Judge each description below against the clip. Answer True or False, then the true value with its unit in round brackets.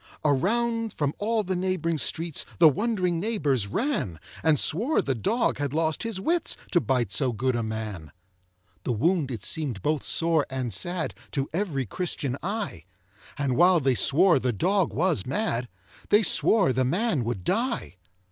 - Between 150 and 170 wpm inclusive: True (165 wpm)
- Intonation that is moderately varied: False (7.1 semitones)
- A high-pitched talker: False (160 Hz)